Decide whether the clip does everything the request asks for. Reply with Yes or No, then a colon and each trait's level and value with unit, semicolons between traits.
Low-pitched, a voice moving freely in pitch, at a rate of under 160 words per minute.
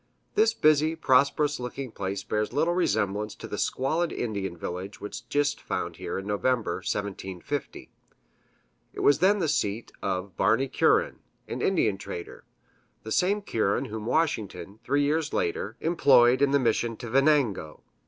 Yes: low, 125 Hz; wide, 6.6 semitones; average, 150 wpm